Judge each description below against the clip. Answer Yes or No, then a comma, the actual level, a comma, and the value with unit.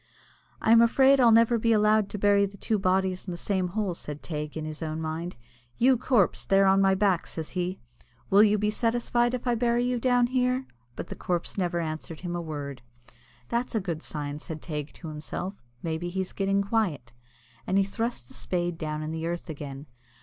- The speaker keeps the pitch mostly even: No, wide, 5.6 semitones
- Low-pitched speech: No, high, 190 Hz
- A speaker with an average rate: No, fast, 210 wpm